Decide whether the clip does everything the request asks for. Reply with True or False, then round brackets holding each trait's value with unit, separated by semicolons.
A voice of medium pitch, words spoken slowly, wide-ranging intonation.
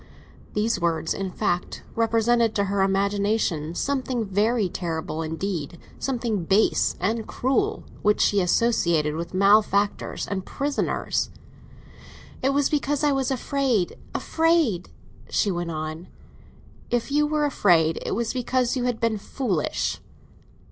False (210 Hz; 125 wpm; 5.9 semitones)